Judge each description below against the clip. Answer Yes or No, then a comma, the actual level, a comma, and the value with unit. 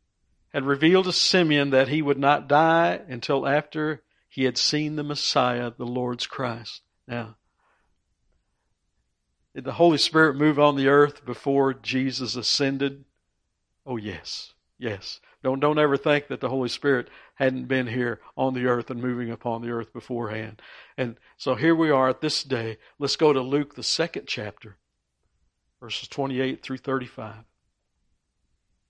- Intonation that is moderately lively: Yes, average, 3.2 semitones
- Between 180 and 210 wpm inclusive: No, average, 155 wpm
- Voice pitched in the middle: No, low, 130 Hz